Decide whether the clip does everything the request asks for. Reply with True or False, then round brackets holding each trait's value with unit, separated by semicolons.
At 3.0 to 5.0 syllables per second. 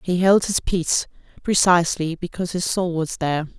False (5.6 syllables/s)